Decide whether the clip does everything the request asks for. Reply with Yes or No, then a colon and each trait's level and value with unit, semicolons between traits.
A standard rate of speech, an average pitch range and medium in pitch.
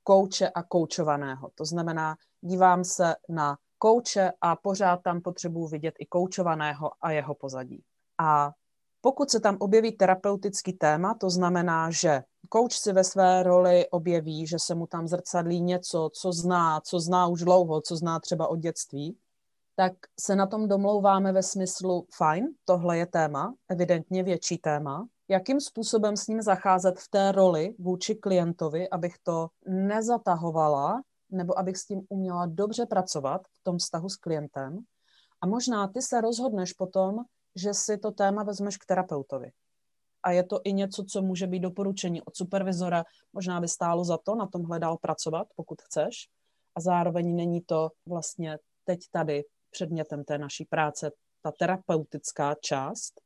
Yes: average, 160 wpm; average, 3.0 semitones; medium, 180 Hz